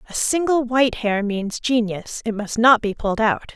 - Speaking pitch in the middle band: No, high, 230 Hz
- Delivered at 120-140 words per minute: No, fast, 205 wpm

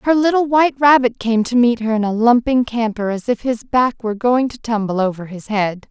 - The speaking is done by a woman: Yes, female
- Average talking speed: No, fast, 235 wpm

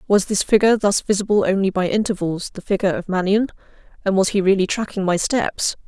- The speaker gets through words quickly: No, average, 195 wpm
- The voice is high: Yes, high, 195 Hz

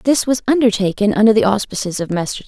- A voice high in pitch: Yes, high, 220 Hz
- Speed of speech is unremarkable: Yes, average, 195 wpm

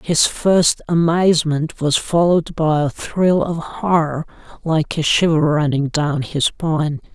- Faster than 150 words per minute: No, average, 145 wpm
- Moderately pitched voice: Yes, medium, 160 Hz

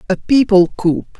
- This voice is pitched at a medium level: No, high, 200 Hz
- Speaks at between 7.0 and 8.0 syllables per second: No, 4.6 syllables/s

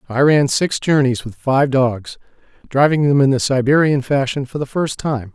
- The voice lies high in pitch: No, low, 135 Hz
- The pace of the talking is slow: No, average, 190 wpm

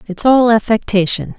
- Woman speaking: Yes, female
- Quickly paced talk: No, slow, 130 wpm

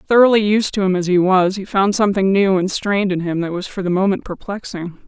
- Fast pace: Yes, fast, 250 wpm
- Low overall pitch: No, high, 190 Hz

